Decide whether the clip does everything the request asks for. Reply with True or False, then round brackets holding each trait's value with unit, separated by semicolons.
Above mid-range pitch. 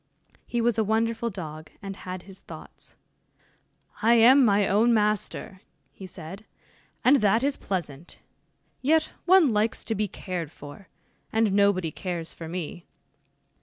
True (200 Hz)